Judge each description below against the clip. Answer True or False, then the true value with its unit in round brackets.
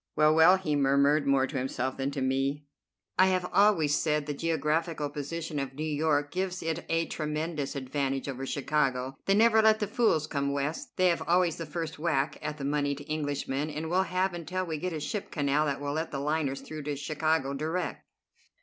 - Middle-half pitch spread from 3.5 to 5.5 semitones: False (3.0 semitones)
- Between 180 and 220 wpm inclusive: True (200 wpm)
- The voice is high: False (150 Hz)